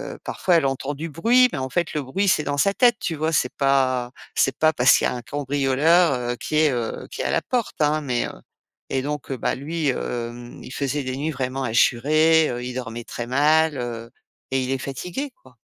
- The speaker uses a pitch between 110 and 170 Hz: Yes, medium, 140 Hz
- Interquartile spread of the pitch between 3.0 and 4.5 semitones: Yes, average, 3.7 semitones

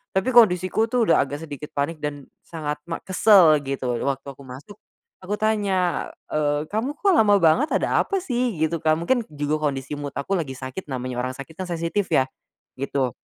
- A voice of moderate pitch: Yes, medium, 160 Hz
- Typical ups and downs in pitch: No, wide, 6.3 semitones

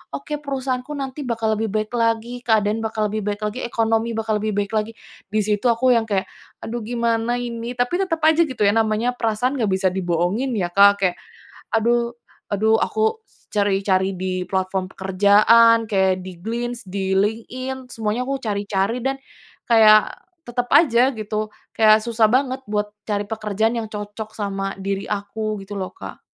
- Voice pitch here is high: Yes, high, 220 Hz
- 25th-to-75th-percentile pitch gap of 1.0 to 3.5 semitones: Yes, average, 2.9 semitones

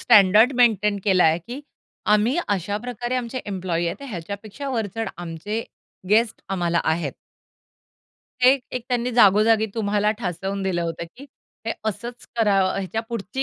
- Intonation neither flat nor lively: Yes, average, 3.9 semitones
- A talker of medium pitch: No, high, 210 Hz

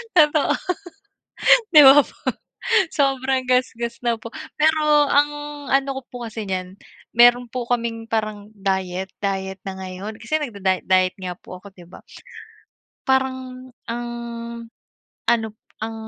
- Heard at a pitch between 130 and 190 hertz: No, high, 235 Hz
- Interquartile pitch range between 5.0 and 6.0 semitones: Yes, average, 5.3 semitones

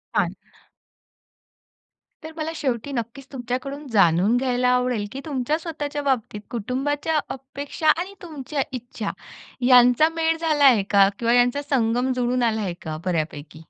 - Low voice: No, very high, 255 Hz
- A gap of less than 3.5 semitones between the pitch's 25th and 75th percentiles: No, average, 3.8 semitones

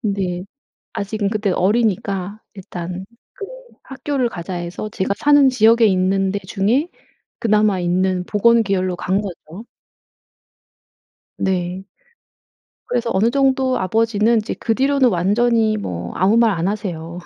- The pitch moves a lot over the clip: No, average, 3.8 semitones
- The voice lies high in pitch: Yes, high, 200 Hz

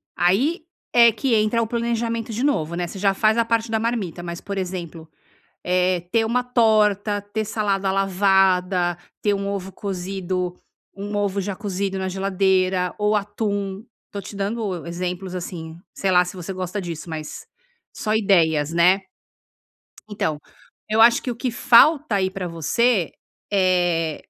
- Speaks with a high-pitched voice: Yes, high, 195 Hz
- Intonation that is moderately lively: Yes, average, 3.2 semitones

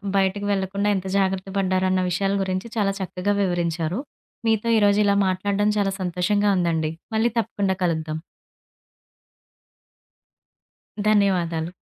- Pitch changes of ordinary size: No, narrow, 2.2 semitones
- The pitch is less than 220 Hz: Yes, high, 190 Hz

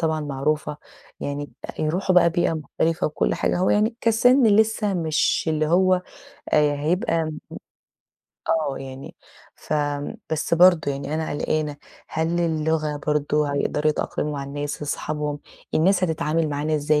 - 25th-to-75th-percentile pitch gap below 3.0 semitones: Yes, narrow, 2.6 semitones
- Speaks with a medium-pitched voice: Yes, medium, 155 Hz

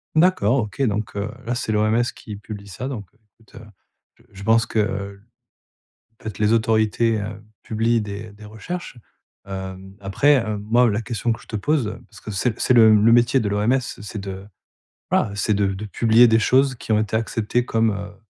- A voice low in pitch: Yes, low, 110 Hz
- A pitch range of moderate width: No, narrow, 2.2 semitones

